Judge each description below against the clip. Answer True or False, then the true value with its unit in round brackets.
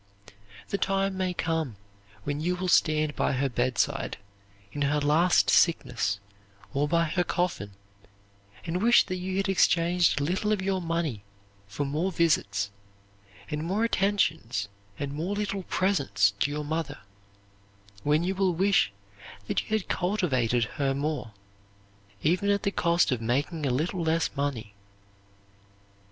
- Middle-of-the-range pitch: True (160 Hz)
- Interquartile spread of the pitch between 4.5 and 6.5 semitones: True (4.8 semitones)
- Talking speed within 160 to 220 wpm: False (145 wpm)